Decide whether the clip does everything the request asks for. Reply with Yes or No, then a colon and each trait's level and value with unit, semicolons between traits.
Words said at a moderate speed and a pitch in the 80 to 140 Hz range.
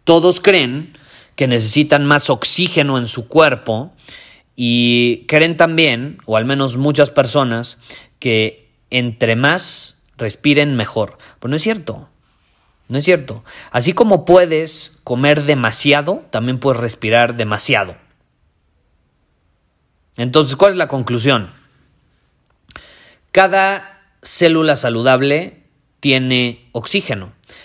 No: slow, 105 wpm; low, 135 Hz